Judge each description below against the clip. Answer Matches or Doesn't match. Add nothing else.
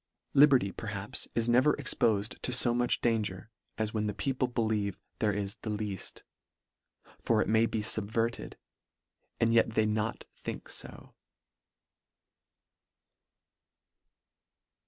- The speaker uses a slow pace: Matches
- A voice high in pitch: Doesn't match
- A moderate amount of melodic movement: Doesn't match